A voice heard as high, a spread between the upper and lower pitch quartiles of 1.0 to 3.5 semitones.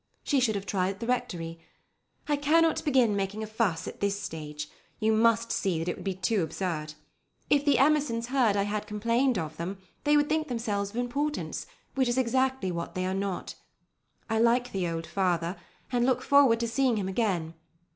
No: high, 220 Hz; average, 5.3 semitones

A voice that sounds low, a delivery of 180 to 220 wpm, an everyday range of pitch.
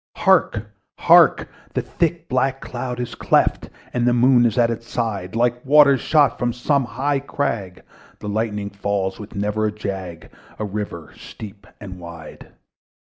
No: low, 115 Hz; average, 150 wpm; average, 3.9 semitones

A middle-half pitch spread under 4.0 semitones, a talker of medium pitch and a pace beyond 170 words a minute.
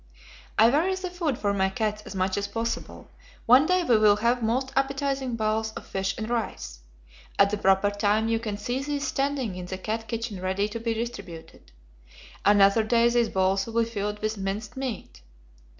No: average, 3.2 semitones; high, 220 Hz; average, 190 wpm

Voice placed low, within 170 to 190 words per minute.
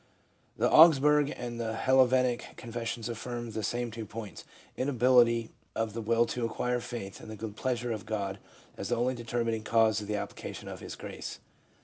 Yes: low, 115 Hz; average, 180 wpm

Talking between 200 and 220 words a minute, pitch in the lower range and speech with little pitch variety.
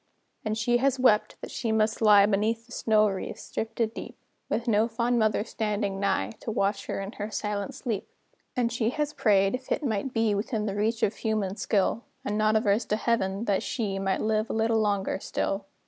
No: fast, 205 wpm; high, 215 Hz; narrow, 2.1 semitones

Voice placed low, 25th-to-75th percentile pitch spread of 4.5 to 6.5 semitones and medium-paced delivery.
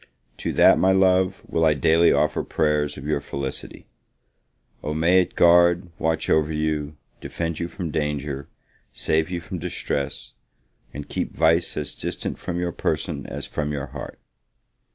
No: very low, 80 Hz; average, 2.8 semitones; average, 155 wpm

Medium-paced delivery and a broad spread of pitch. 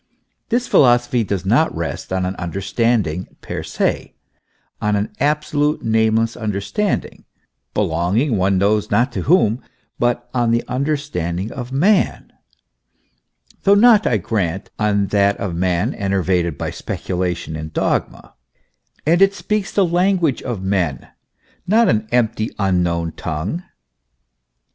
No: slow, 125 wpm; wide, 7.1 semitones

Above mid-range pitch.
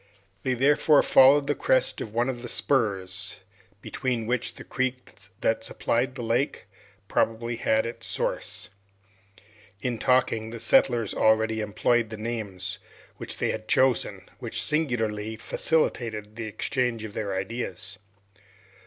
No: low, 115 Hz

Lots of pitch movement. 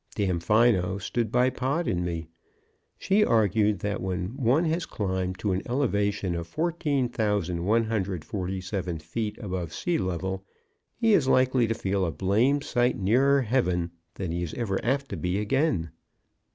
Yes: wide, 5.7 semitones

